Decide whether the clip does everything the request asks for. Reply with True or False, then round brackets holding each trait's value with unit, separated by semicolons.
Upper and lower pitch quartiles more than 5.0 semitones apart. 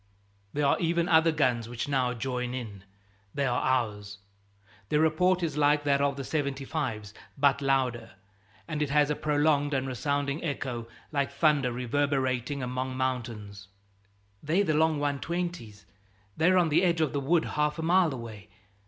False (3.5 semitones)